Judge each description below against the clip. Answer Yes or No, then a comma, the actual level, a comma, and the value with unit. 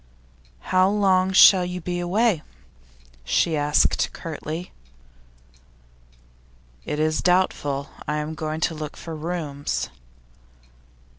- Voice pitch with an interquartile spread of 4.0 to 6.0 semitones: No, average, 3.2 semitones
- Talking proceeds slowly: Yes, slow, 100 wpm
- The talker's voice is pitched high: No, medium, 165 Hz